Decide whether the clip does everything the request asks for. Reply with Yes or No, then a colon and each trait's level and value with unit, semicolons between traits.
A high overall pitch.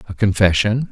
No: low, 105 Hz